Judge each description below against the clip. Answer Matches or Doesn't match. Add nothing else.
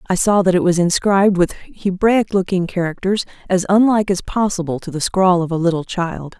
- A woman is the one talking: Matches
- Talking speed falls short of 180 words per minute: Doesn't match